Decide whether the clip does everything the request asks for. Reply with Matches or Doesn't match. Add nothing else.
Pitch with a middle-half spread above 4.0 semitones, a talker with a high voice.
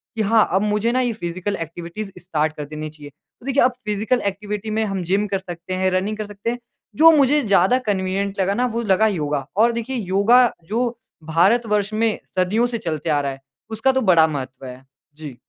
Matches